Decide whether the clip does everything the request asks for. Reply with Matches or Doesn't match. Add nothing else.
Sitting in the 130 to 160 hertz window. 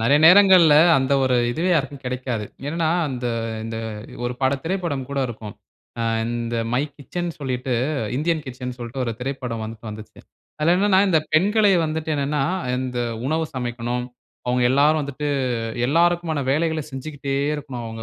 Matches